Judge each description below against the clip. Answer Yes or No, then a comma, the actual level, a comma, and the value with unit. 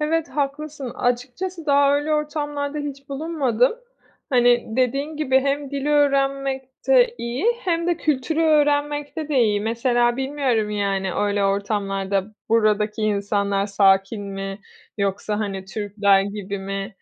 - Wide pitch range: Yes, wide, 6.1 semitones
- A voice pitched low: No, very high, 255 Hz